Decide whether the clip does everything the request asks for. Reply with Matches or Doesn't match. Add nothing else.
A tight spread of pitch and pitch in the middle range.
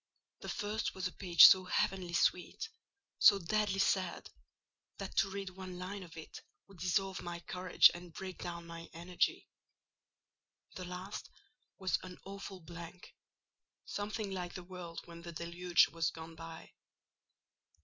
Matches